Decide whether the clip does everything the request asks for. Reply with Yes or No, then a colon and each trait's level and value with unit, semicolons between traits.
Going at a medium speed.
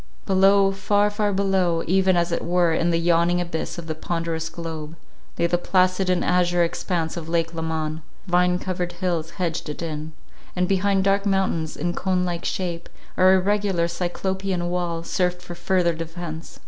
Yes: average, 170 wpm